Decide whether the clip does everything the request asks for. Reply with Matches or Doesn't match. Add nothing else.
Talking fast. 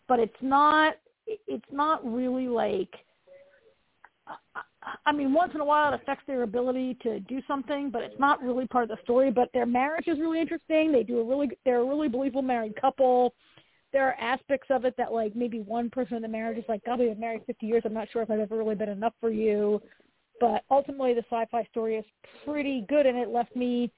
Matches